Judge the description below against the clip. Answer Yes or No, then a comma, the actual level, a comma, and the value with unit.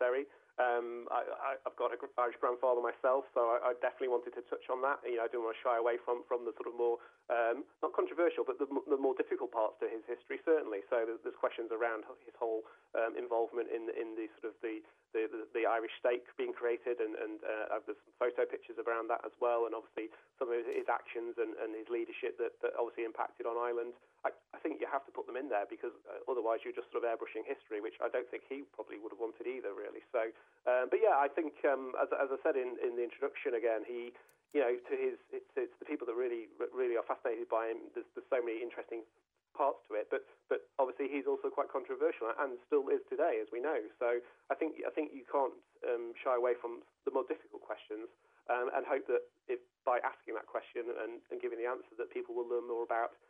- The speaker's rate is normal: No, fast, 240 wpm